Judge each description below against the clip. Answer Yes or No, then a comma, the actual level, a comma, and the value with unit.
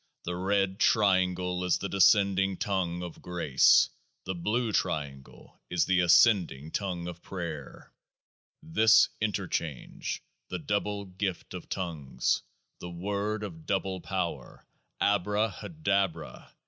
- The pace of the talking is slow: Yes, slow, 115 wpm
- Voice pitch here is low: Yes, very low, 95 Hz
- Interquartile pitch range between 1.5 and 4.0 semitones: Yes, average, 2.8 semitones